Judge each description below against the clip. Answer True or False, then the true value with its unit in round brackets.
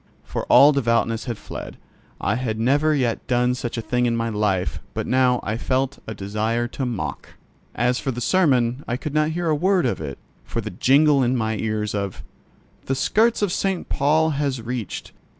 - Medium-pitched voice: False (125 Hz)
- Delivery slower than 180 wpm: False (195 wpm)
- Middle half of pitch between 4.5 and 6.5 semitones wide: False (4.1 semitones)